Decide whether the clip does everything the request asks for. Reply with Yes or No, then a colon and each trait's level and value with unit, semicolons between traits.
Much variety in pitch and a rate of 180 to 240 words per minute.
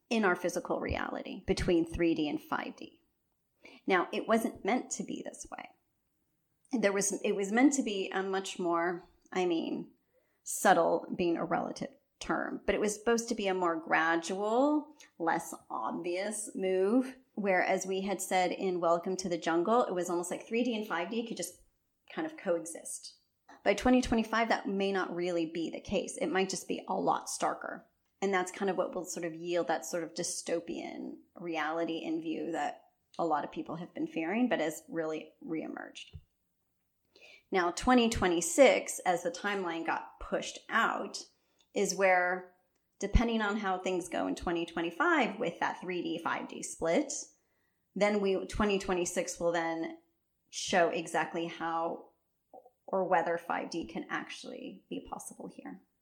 No: wide, 5.7 semitones; average, 160 wpm